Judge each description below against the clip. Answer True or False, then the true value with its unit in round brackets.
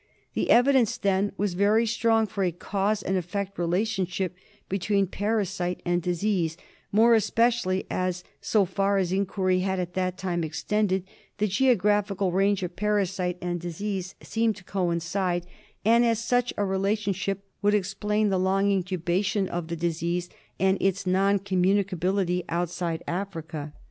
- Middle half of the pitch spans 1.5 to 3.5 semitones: True (2.4 semitones)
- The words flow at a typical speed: True (145 wpm)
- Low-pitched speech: False (195 Hz)